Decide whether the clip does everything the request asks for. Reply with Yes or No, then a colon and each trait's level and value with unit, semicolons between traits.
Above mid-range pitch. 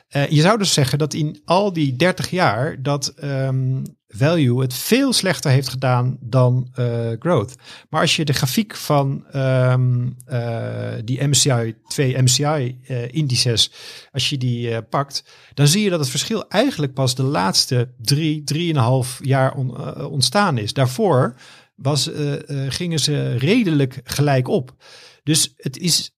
No: medium, 140 Hz